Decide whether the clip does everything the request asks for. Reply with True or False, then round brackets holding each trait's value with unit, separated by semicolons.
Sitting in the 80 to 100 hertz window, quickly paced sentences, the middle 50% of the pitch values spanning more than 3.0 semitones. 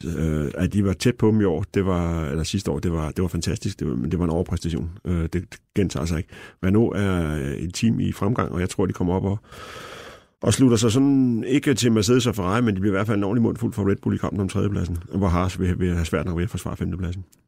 True (95 Hz; 280 wpm; 3.9 semitones)